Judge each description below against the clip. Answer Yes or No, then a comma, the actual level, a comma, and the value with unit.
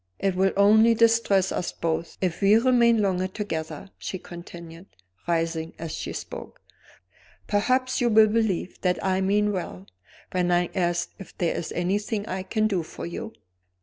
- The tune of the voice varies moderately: Yes, average, 3.9 semitones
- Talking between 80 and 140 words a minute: No, average, 160 wpm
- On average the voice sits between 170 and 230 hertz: Yes, high, 190 Hz